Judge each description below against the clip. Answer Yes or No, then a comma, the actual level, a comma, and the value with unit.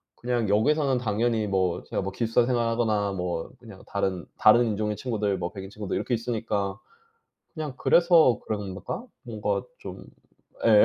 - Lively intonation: No, average, 3.5 semitones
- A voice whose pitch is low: Yes, low, 110 Hz